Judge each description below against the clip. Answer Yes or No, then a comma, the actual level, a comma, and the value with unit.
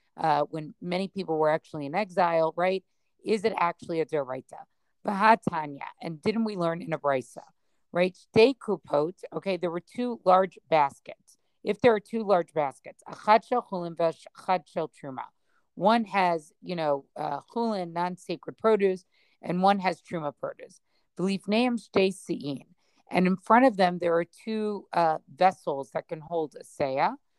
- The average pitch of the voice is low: No, medium, 180 Hz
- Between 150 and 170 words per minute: Yes, average, 160 wpm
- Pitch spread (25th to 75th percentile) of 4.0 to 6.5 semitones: Yes, average, 4.3 semitones